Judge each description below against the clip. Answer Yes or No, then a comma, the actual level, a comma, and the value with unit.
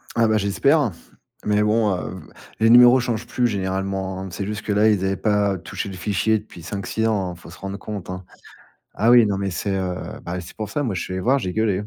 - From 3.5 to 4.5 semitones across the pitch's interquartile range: No, average, 2.8 semitones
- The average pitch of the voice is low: Yes, low, 100 Hz